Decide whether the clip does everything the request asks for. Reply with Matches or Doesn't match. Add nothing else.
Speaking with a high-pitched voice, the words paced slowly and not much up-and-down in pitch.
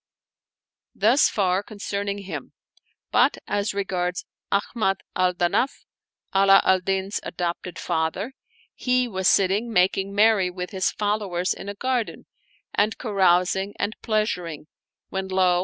Matches